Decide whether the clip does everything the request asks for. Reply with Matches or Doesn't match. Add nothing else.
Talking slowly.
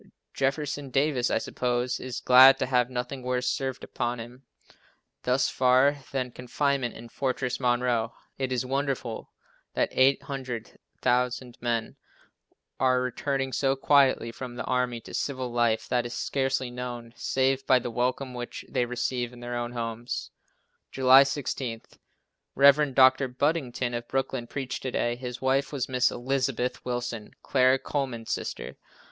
Doesn't match